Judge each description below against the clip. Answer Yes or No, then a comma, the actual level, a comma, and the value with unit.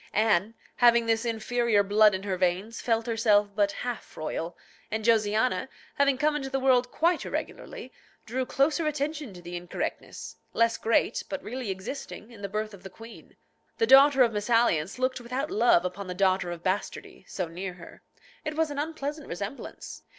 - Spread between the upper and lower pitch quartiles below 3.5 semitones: No, average, 4.8 semitones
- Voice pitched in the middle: No, high, 225 Hz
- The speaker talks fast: No, average, 175 wpm